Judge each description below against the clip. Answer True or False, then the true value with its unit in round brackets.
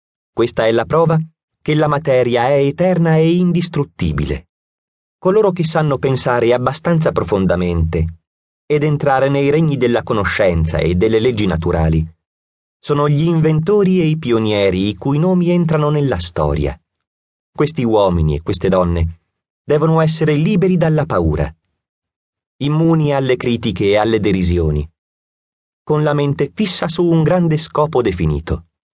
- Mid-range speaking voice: False (125 Hz)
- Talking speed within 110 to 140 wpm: True (135 wpm)